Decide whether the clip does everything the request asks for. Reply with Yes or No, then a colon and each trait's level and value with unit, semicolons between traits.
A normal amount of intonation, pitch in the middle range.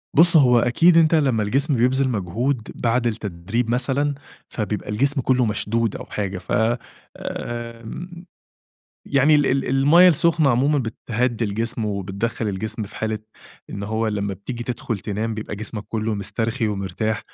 No: average, 4.1 semitones; low, 115 Hz